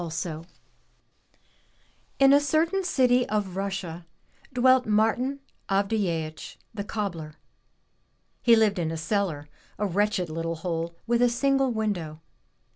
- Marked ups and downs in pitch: Yes, wide, 6.6 semitones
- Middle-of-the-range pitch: No, high, 205 Hz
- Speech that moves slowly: Yes, slow, 120 wpm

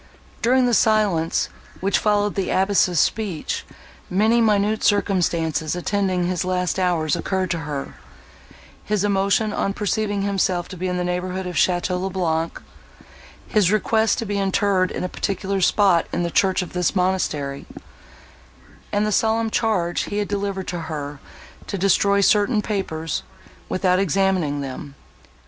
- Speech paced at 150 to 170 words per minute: No, average, 140 wpm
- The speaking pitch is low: No, high, 190 Hz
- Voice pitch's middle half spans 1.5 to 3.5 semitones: Yes, average, 2.7 semitones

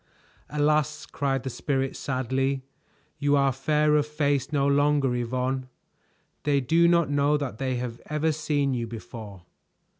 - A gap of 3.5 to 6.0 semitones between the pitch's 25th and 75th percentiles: No, narrow, 2.4 semitones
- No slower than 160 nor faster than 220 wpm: No, average, 145 wpm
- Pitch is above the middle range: No, medium, 140 Hz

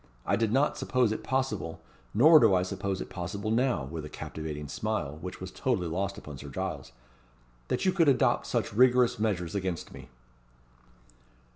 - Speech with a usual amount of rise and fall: No, wide, 6.6 semitones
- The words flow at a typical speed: Yes, average, 170 wpm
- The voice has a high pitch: No, low, 100 Hz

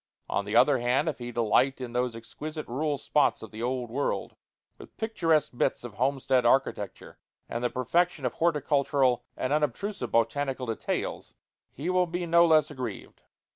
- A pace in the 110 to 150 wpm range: No, average, 165 wpm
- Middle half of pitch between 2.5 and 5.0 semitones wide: Yes, average, 4.1 semitones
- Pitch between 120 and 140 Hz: Yes, low, 135 Hz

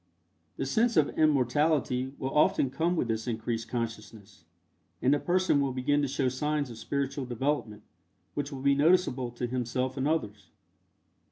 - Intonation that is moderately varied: Yes, average, 3.3 semitones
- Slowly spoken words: No, average, 160 wpm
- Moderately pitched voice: No, low, 130 Hz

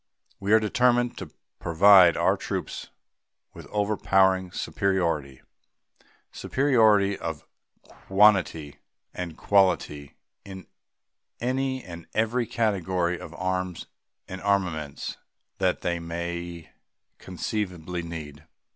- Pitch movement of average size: Yes, average, 3.5 semitones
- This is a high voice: No, very low, 95 Hz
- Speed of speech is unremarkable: No, slow, 95 wpm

